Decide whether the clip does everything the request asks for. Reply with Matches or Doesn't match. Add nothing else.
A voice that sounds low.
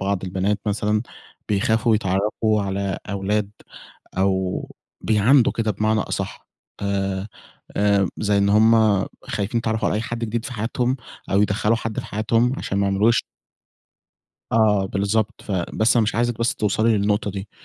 Matches